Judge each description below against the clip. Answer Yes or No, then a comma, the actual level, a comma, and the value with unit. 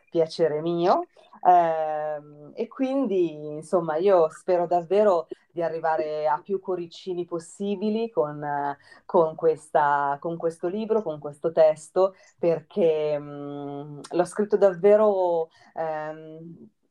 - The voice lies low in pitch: No, medium, 165 Hz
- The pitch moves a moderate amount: Yes, average, 3.5 semitones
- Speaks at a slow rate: Yes, slow, 95 wpm